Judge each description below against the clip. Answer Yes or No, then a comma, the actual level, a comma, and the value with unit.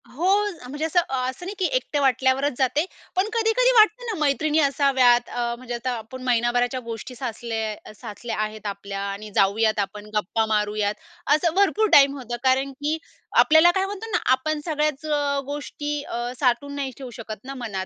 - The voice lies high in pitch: Yes, very high, 265 Hz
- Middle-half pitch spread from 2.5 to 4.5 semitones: No, average, 5.1 semitones